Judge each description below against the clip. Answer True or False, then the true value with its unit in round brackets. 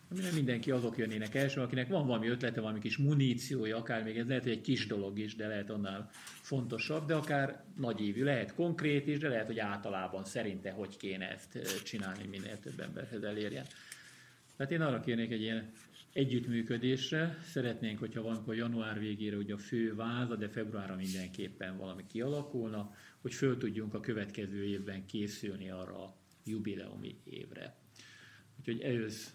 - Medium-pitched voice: False (115 Hz)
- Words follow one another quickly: True (160 wpm)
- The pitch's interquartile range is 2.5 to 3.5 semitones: False (4.1 semitones)